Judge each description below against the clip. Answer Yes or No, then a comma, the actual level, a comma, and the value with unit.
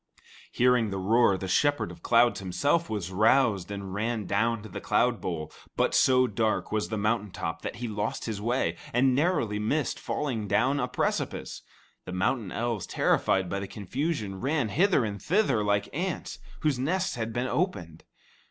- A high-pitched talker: No, low, 110 Hz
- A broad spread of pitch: No, average, 4.5 semitones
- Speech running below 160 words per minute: No, average, 170 wpm